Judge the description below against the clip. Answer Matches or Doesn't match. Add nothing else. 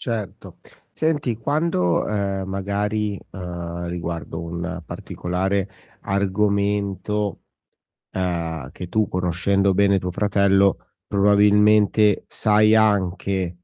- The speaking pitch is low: Matches